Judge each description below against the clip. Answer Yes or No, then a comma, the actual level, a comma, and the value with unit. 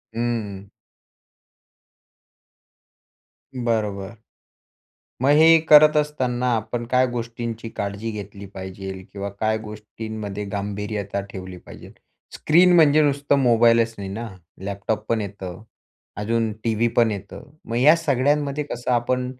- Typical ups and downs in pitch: Yes, average, 3.8 semitones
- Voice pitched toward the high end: No, low, 115 Hz